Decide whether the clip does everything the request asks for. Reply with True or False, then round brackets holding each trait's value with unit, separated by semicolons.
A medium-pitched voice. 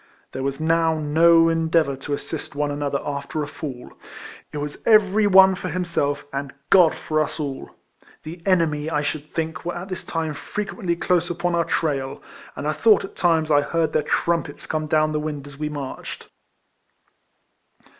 True (155 Hz)